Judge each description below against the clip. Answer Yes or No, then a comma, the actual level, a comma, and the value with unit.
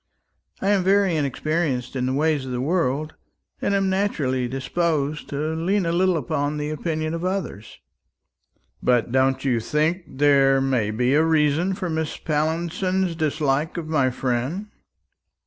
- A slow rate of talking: No, average, 150 wpm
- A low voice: No, medium, 155 Hz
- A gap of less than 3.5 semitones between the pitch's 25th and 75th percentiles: No, average, 4.2 semitones